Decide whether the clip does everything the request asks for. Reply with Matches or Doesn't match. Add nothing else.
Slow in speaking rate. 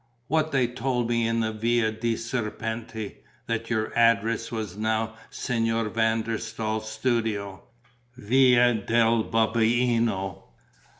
Matches